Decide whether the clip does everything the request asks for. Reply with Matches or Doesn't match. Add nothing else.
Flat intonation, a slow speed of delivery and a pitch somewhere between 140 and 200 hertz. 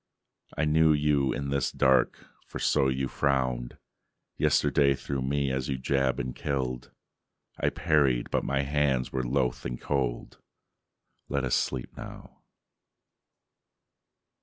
Doesn't match